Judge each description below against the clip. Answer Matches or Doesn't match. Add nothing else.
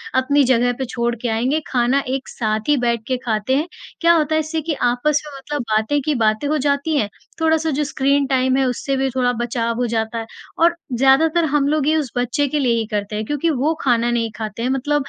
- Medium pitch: Doesn't match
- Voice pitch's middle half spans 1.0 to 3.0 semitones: Doesn't match